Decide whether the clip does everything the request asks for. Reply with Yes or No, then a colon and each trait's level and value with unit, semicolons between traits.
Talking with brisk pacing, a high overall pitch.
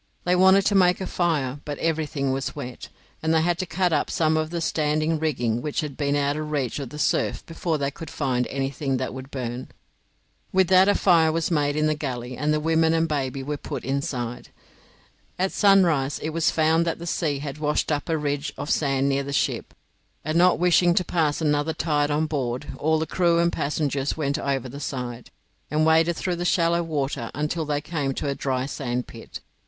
No: fast, 210 wpm; medium, 150 Hz